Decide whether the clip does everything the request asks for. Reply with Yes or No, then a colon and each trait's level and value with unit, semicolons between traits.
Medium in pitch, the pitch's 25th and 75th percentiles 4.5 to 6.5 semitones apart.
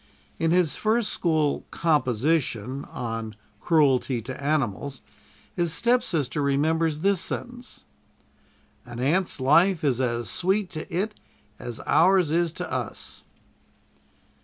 Yes: medium, 155 Hz; average, 5.2 semitones